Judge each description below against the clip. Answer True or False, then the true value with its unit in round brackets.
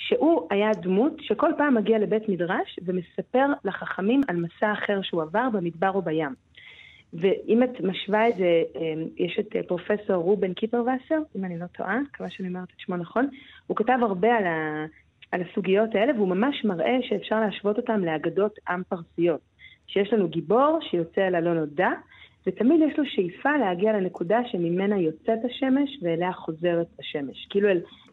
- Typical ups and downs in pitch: True (4.7 semitones)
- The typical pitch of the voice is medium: False (200 Hz)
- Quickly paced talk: True (160 wpm)